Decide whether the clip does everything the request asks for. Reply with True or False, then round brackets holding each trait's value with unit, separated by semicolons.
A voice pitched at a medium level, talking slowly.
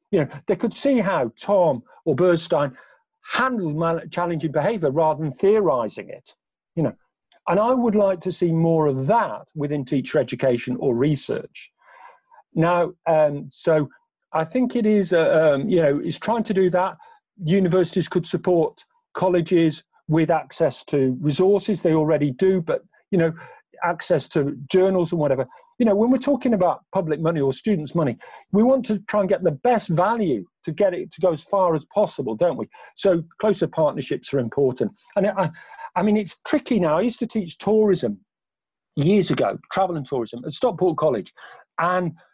False (180 Hz; 175 wpm)